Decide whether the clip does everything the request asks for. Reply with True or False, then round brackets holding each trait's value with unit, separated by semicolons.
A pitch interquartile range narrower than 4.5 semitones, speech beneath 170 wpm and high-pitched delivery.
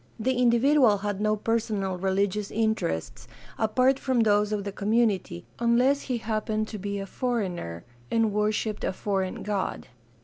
True (2.7 semitones; 145 wpm; 215 Hz)